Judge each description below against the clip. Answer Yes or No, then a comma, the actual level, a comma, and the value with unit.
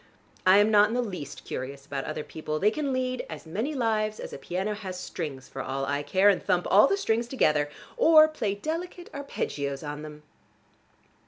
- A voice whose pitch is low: No, high, 200 Hz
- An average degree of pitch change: No, wide, 8.4 semitones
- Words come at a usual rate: Yes, average, 195 wpm